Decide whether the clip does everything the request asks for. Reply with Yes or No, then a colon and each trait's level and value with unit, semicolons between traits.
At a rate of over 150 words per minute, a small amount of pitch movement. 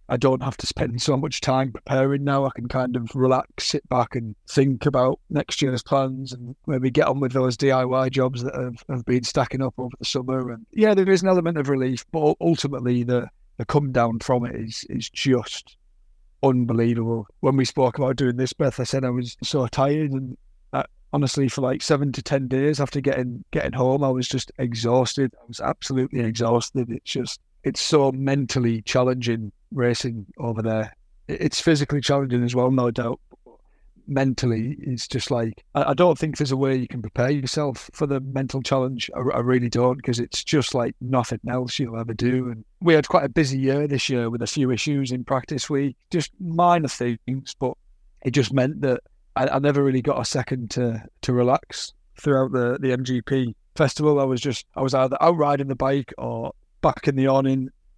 Yes: average, 200 wpm; narrow, 2.1 semitones